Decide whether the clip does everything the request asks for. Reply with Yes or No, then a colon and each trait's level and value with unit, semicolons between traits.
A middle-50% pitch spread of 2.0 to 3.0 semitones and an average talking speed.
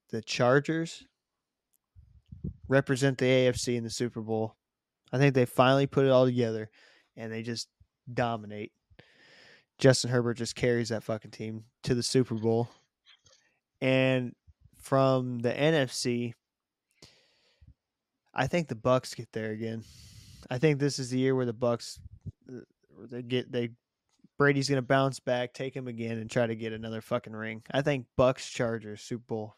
Yes: narrow, 2.6 semitones; average, 150 wpm